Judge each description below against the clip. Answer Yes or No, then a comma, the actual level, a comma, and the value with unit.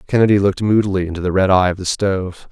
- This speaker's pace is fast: Yes, fast, 240 wpm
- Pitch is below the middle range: Yes, very low, 95 Hz